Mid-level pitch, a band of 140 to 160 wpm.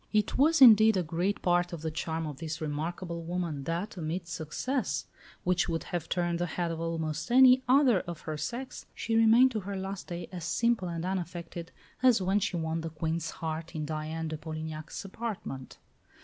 No: medium, 175 Hz; average, 190 wpm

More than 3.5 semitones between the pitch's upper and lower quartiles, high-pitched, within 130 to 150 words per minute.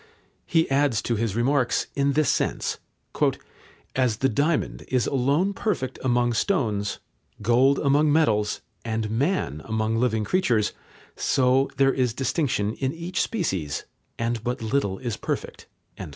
No: average, 4.1 semitones; low, 125 Hz; slow, 135 wpm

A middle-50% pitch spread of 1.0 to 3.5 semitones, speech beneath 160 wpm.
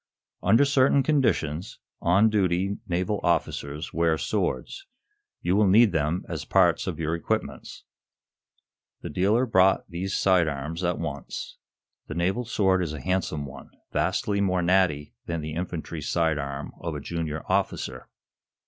No: average, 4.0 semitones; average, 145 wpm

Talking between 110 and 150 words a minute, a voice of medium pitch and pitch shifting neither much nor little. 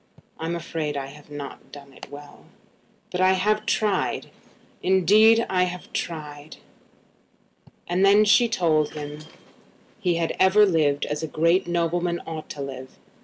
Yes: average, 140 wpm; medium, 170 Hz; average, 4.2 semitones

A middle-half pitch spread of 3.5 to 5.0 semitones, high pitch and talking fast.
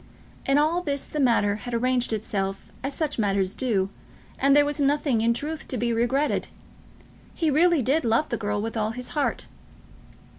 No: average, 4.7 semitones; very high, 250 Hz; average, 180 wpm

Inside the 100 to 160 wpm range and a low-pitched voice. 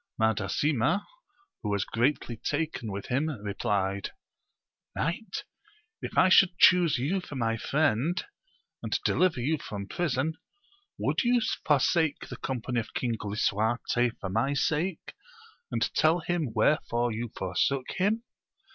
Yes: slow, 135 wpm; low, 130 Hz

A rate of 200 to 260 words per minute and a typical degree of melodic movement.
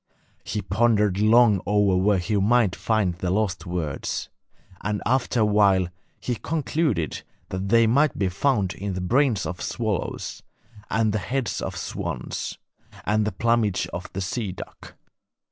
No: average, 150 wpm; average, 3.7 semitones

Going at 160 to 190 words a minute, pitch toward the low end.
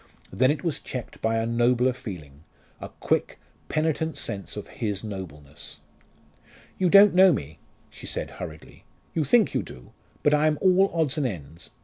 Yes: average, 165 wpm; low, 125 Hz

